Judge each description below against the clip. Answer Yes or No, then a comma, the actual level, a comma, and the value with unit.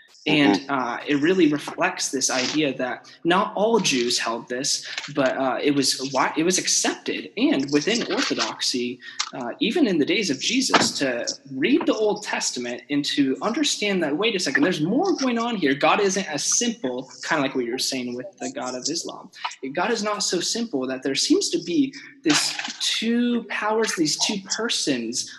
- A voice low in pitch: No, medium, 180 Hz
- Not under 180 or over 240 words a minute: Yes, average, 185 wpm